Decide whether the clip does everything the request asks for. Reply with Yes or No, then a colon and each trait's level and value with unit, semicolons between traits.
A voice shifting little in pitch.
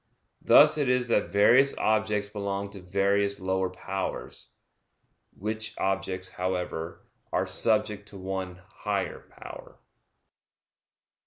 Yes: narrow, 2.3 semitones